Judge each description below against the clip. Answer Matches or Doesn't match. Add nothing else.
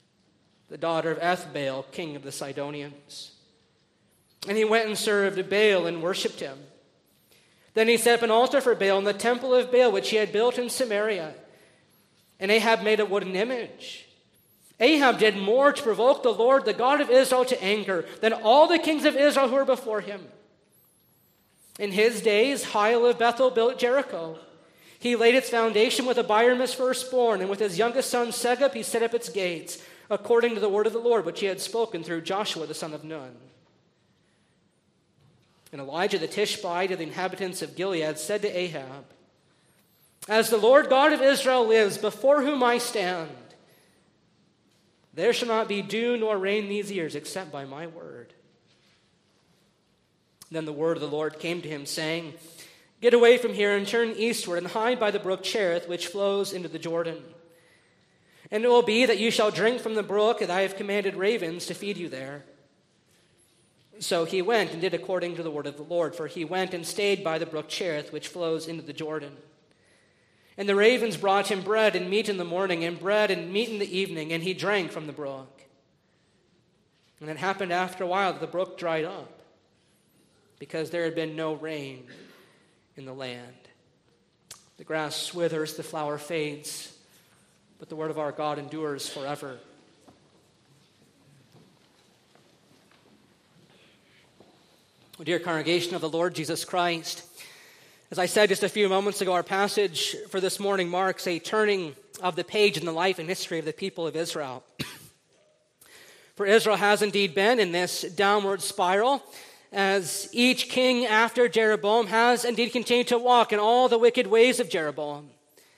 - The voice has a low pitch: Doesn't match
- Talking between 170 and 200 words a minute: Matches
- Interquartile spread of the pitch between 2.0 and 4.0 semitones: Doesn't match